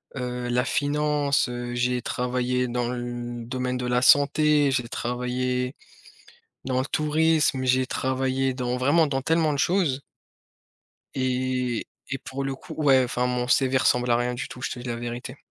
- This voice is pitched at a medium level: No, low, 125 Hz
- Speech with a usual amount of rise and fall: No, narrow, 1.7 semitones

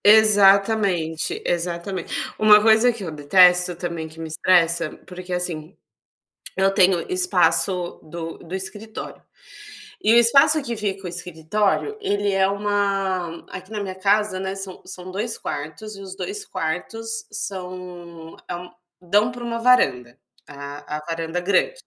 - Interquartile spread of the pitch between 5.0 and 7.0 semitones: No, average, 3.6 semitones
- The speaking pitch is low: No, high, 190 Hz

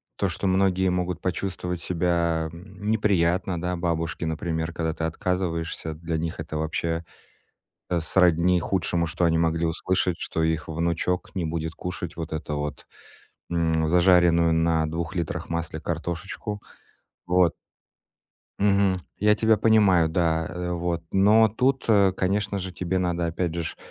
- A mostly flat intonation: Yes, narrow, 2.2 semitones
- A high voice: No, very low, 85 Hz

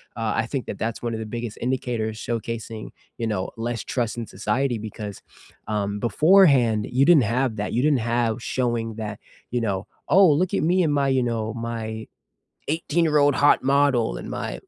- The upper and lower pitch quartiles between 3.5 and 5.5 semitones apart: Yes, average, 3.8 semitones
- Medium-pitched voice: No, low, 120 Hz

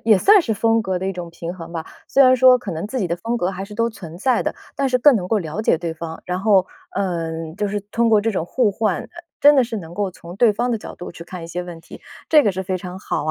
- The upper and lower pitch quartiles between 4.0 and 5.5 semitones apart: Yes, average, 4.8 semitones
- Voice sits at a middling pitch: No, high, 195 Hz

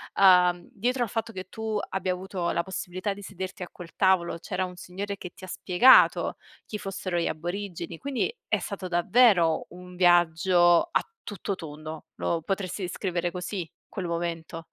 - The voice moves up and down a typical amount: No, narrow, 2.3 semitones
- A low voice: No, medium, 180 Hz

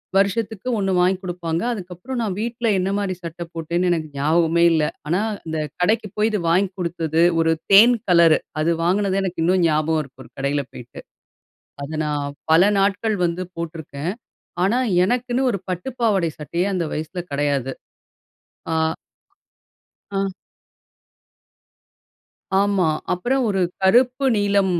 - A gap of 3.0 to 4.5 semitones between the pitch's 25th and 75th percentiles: Yes, average, 3.8 semitones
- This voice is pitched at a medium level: Yes, medium, 180 Hz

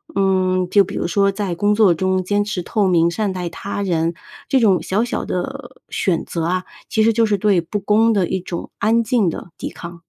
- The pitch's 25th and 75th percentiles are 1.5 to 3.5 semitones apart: Yes, average, 3.2 semitones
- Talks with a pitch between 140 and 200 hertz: Yes, high, 195 Hz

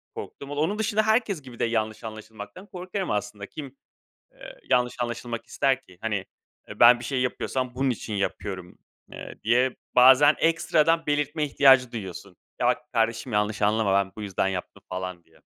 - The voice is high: No, low, 120 Hz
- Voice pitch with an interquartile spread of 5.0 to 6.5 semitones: Yes, wide, 5.5 semitones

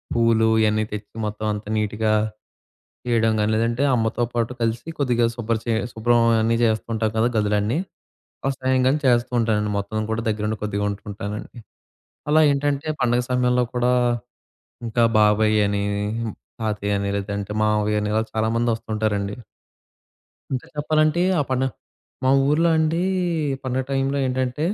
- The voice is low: Yes, low, 115 Hz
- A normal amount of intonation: Yes, average, 3.0 semitones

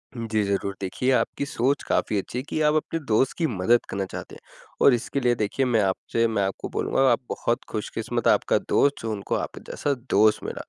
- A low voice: Yes, low, 115 Hz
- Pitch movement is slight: No, average, 4.3 semitones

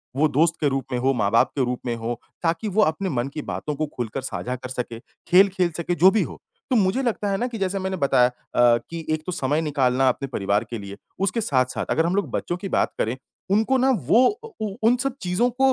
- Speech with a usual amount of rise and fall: No, wide, 7.5 semitones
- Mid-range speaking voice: Yes, medium, 160 Hz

